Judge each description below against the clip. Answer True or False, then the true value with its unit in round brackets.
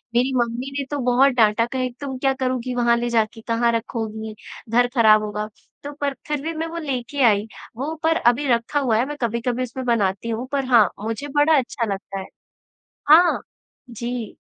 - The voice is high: True (245 Hz)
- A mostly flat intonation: False (3.1 semitones)